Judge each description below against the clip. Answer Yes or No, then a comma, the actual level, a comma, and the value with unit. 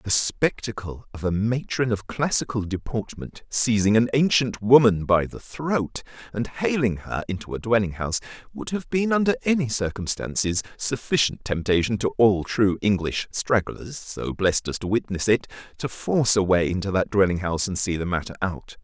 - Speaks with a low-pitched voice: Yes, low, 110 Hz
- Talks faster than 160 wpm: Yes, average, 170 wpm